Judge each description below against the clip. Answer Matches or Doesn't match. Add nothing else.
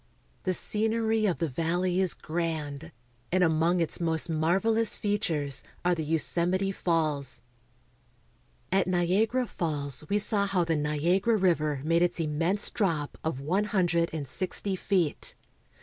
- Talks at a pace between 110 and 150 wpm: Matches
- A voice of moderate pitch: Matches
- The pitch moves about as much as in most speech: Matches